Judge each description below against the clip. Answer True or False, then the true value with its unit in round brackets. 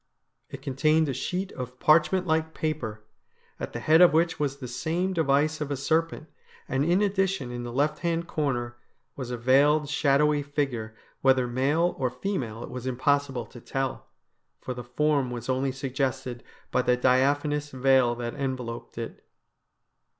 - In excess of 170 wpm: False (165 wpm)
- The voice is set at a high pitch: False (135 Hz)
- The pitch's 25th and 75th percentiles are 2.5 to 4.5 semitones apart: True (3.5 semitones)